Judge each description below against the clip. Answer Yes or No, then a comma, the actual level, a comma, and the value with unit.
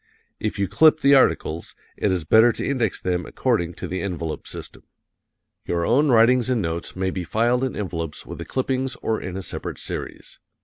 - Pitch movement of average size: No, wide, 6.2 semitones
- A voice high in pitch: No, low, 105 Hz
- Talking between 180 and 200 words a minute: Yes, average, 190 wpm